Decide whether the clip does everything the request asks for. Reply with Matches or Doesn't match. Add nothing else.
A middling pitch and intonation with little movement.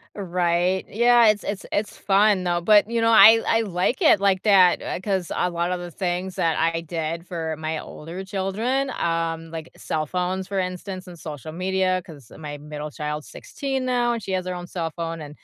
Doesn't match